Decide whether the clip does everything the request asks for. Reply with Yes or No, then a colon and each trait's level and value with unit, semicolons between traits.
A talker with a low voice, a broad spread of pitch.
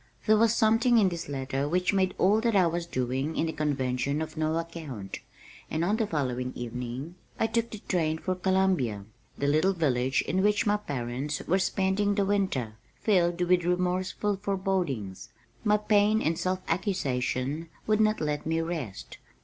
No: medium, 170 Hz; wide, 6.0 semitones